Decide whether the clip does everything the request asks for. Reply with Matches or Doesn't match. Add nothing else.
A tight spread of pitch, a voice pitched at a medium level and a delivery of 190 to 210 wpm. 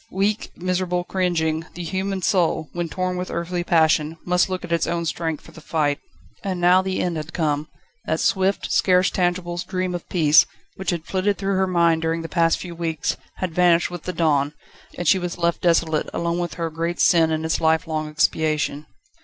Matches